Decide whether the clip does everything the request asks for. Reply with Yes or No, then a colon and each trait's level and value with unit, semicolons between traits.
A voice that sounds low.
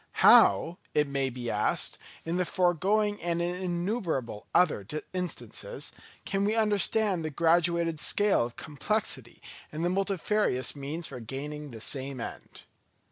No: medium, 170 Hz